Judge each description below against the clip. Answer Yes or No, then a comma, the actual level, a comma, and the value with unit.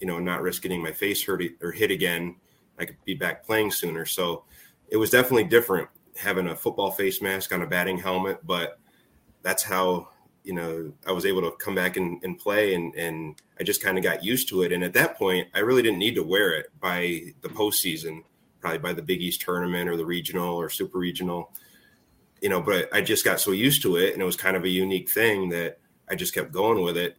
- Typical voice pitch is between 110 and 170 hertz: No, very low, 90 Hz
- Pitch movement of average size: No, narrow, 1.5 semitones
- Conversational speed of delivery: No, fast, 235 wpm